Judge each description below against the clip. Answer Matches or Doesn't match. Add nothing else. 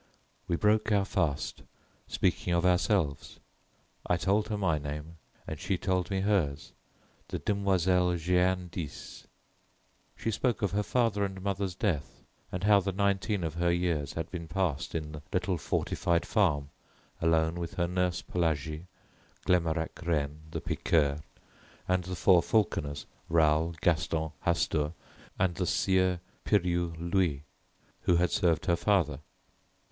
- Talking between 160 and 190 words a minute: Doesn't match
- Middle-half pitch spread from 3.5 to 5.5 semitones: Doesn't match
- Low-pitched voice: Matches